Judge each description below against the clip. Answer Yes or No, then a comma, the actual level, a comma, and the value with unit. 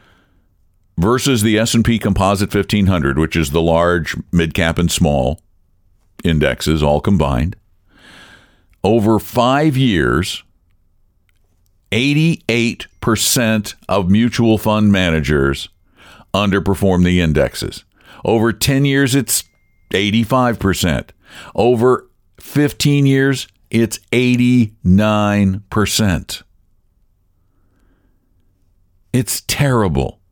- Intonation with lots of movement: No, average, 4.5 semitones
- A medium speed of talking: No, slow, 95 wpm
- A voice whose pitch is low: Yes, very low, 95 Hz